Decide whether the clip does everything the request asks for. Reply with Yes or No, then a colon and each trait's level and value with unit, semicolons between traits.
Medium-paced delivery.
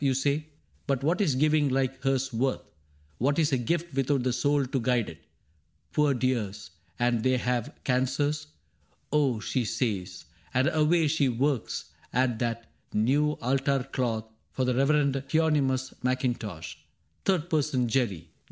Yes: average, 160 wpm